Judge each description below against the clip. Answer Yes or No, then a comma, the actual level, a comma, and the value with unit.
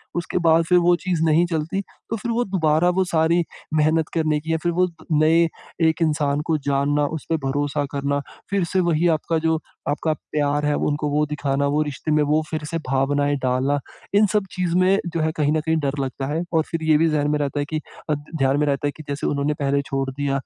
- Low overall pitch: No, medium, 155 Hz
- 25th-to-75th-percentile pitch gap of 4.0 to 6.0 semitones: No, narrow, 2.5 semitones